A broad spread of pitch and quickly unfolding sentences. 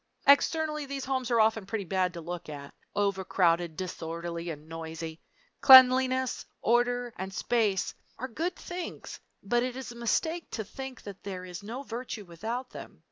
No: wide, 6.4 semitones; average, 160 wpm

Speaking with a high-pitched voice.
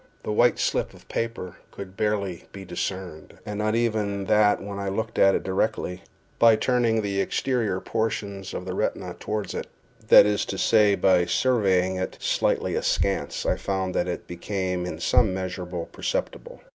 No: low, 100 Hz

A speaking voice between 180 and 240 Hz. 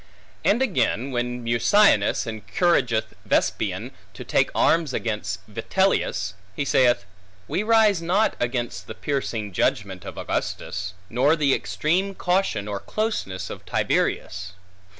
No: low, 125 Hz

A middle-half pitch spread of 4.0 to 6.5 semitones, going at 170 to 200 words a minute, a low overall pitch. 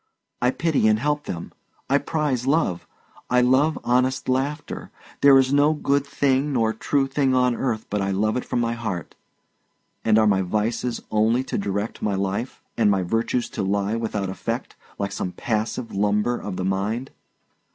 Yes: average, 4.5 semitones; average, 175 wpm; low, 115 Hz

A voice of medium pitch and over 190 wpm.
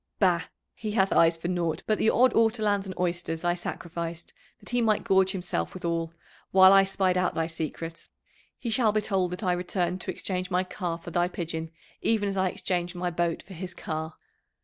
Yes: medium, 180 Hz; average, 200 wpm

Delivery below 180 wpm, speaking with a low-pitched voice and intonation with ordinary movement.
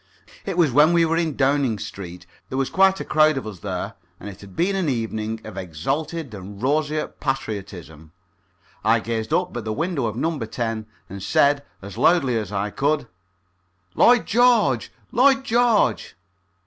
No: average, 170 wpm; low, 130 Hz; wide, 7.6 semitones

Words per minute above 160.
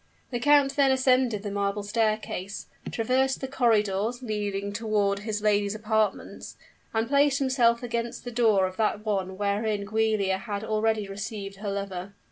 No: average, 150 wpm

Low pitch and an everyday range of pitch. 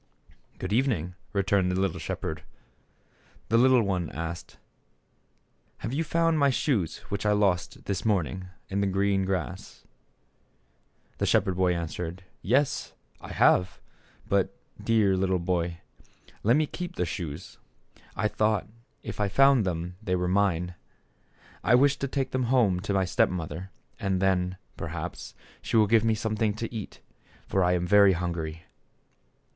Yes: very low, 95 Hz; average, 3.8 semitones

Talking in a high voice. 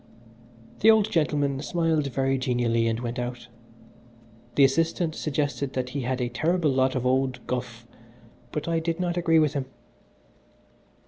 No: low, 135 Hz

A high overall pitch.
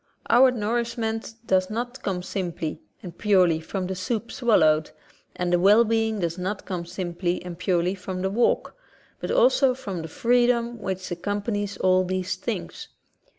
Yes: high, 195 Hz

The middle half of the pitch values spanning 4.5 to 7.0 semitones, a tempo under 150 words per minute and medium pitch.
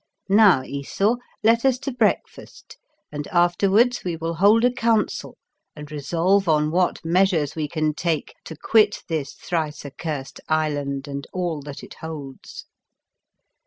Yes: average, 5.2 semitones; average, 140 wpm; medium, 165 Hz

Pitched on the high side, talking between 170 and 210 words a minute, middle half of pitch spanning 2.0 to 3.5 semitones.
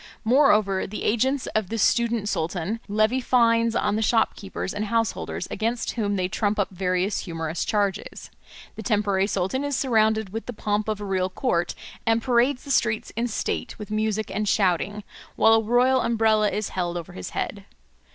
Yes: high, 215 Hz; average, 175 wpm; average, 2.8 semitones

